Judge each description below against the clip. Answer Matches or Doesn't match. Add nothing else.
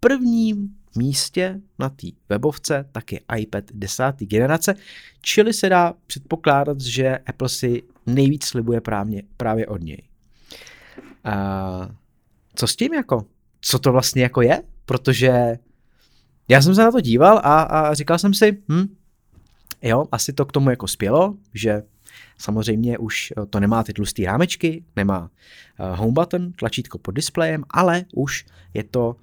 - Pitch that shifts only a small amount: Doesn't match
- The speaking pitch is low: Matches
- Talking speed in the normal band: Matches